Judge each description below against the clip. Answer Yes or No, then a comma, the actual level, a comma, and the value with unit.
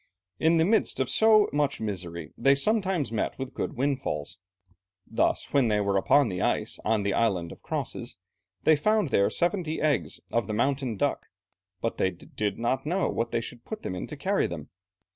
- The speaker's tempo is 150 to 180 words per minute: No, average, 190 wpm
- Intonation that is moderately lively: No, wide, 7.6 semitones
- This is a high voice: No, low, 130 Hz